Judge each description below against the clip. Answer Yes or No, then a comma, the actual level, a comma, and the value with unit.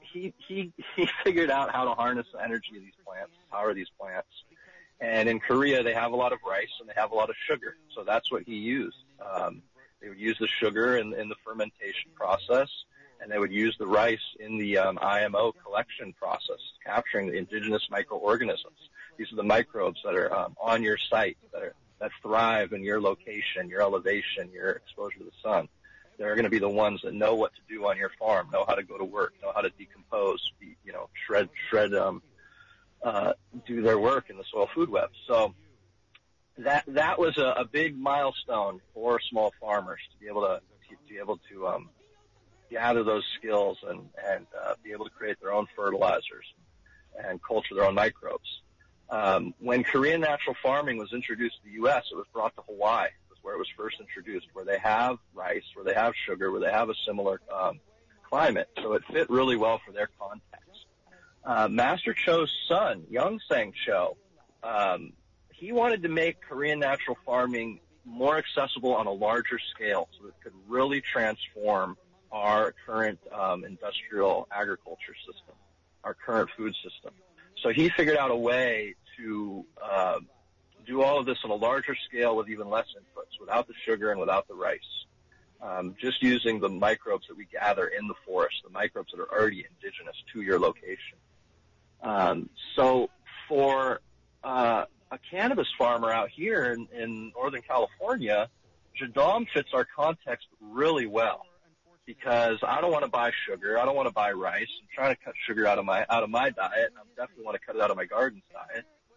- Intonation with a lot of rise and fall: Yes, wide, 8.3 semitones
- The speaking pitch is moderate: No, low, 120 Hz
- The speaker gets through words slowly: No, average, 190 wpm